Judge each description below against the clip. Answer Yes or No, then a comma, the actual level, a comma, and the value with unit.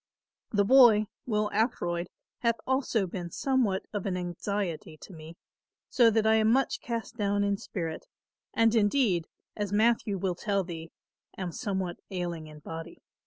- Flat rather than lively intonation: No, average, 4.3 semitones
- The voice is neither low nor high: No, high, 200 Hz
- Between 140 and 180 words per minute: Yes, average, 155 wpm